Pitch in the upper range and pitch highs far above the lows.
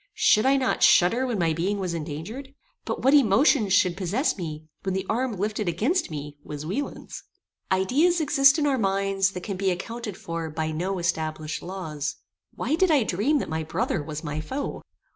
Yes: high, 195 Hz; wide, 7.4 semitones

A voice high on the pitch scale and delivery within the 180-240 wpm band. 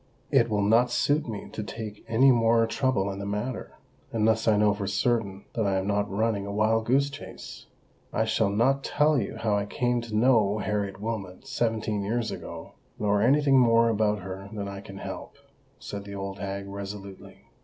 No: low, 105 Hz; average, 195 wpm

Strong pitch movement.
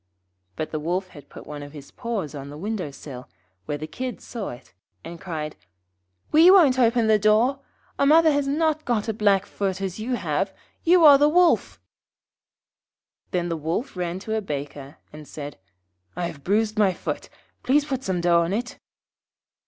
Yes: wide, 8.4 semitones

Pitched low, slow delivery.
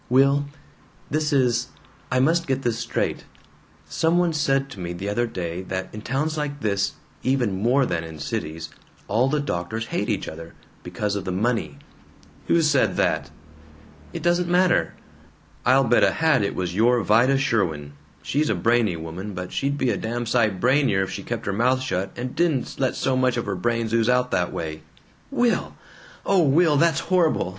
No: low, 120 Hz; average, 185 wpm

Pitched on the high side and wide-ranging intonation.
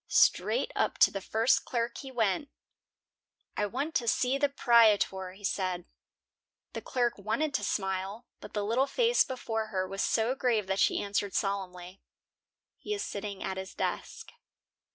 No: high, 215 Hz; average, 4.5 semitones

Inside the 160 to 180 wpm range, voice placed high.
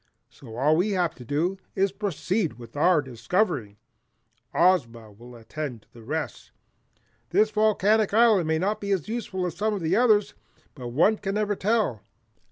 No: average, 175 wpm; medium, 180 Hz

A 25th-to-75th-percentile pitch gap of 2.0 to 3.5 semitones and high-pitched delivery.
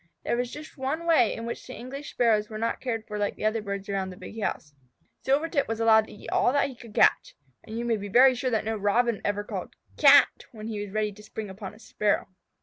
Yes: average, 3.0 semitones; high, 225 Hz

